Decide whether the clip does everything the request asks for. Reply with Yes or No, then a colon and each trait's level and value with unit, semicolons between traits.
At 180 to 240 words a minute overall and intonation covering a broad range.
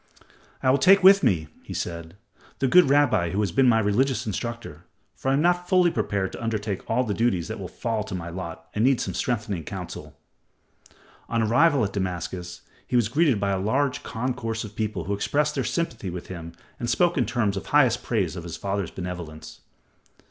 Yes: average, 200 wpm; wide, 6.1 semitones